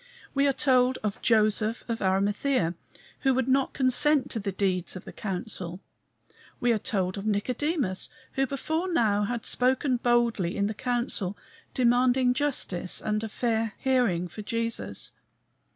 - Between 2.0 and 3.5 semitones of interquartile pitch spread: No, average, 4.2 semitones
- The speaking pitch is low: No, high, 230 Hz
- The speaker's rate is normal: Yes, average, 150 wpm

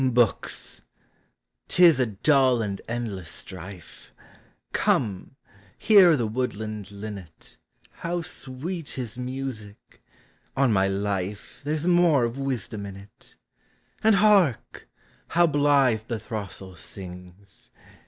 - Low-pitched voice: Yes, low, 115 Hz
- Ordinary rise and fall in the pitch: No, wide, 6.1 semitones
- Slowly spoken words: Yes, slow, 115 wpm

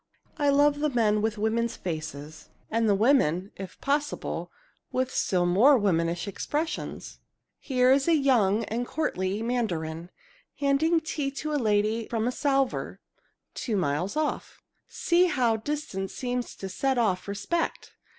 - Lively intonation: Yes, wide, 6.2 semitones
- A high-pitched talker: Yes, high, 235 Hz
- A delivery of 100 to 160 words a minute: Yes, average, 140 wpm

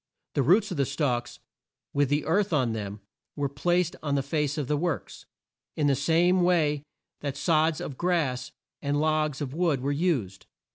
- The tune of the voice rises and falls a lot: No, average, 3.2 semitones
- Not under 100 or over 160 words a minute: No, average, 180 wpm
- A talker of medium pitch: Yes, medium, 150 Hz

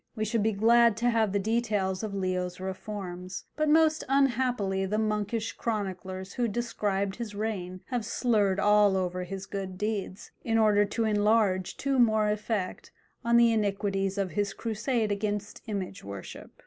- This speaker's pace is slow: No, average, 160 wpm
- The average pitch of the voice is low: No, high, 210 Hz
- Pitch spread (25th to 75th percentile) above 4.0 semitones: No, average, 2.8 semitones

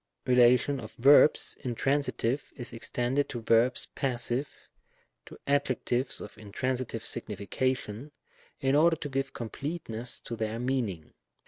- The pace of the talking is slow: Yes, slow, 120 wpm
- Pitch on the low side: Yes, low, 125 Hz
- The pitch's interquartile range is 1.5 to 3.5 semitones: Yes, average, 2.9 semitones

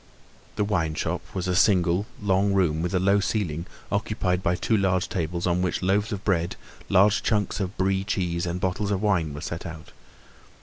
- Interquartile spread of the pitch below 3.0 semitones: Yes, narrow, 2.6 semitones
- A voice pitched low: Yes, very low, 95 Hz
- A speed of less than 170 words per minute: No, average, 190 wpm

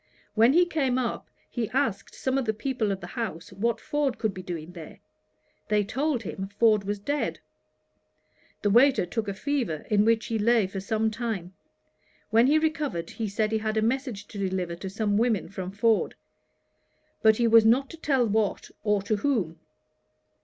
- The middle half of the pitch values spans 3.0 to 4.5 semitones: Yes, average, 3.7 semitones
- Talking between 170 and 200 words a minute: Yes, average, 185 wpm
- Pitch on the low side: No, high, 220 Hz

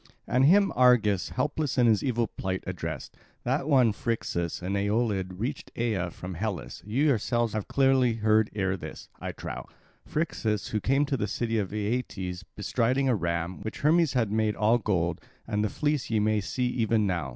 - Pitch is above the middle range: No, low, 110 Hz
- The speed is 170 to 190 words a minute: Yes, average, 180 wpm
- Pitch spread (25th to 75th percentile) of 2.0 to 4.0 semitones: No, average, 4.5 semitones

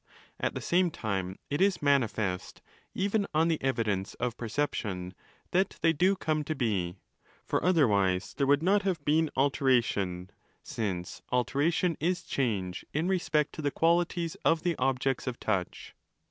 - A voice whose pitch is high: No, medium, 140 Hz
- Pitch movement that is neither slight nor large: No, wide, 7.7 semitones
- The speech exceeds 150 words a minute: Yes, average, 160 wpm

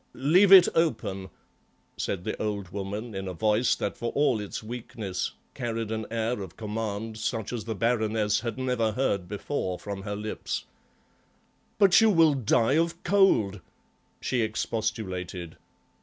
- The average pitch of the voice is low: Yes, low, 110 Hz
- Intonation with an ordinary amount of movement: Yes, average, 3.6 semitones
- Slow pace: No, average, 145 wpm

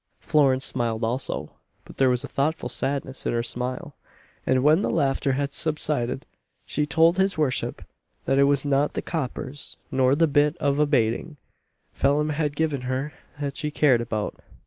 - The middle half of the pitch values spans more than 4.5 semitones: No, narrow, 2.6 semitones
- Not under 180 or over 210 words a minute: No, average, 170 wpm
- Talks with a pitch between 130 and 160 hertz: Yes, medium, 140 Hz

